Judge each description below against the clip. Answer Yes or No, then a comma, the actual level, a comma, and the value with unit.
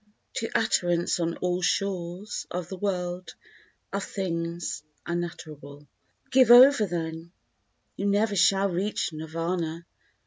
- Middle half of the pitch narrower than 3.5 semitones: Yes, average, 2.9 semitones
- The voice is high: No, medium, 175 Hz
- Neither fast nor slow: No, slow, 110 wpm